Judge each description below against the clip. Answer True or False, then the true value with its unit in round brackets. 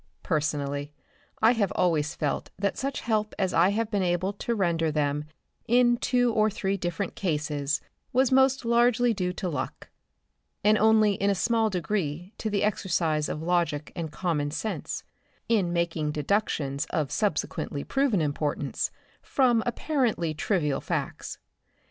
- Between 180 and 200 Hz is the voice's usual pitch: True (185 Hz)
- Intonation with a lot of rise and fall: True (6.2 semitones)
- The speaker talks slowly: False (145 wpm)